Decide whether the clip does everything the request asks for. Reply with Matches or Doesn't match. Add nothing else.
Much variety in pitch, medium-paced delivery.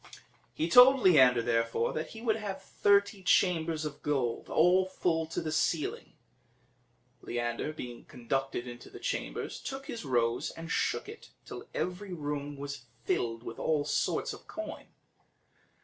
Matches